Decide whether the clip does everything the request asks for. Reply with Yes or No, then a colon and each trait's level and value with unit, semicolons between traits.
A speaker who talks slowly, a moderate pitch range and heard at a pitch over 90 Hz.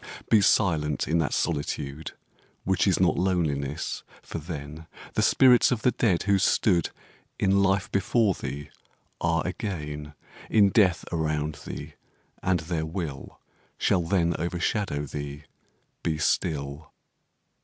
No: slow, 120 wpm; average, 4.3 semitones; very low, 85 Hz